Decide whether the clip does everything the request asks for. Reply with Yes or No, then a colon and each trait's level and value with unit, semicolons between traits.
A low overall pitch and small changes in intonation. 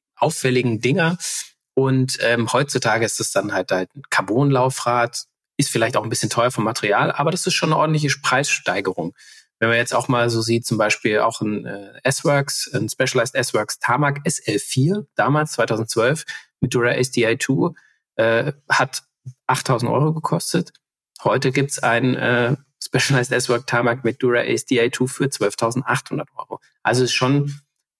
No: low, 125 Hz; average, 3.0 semitones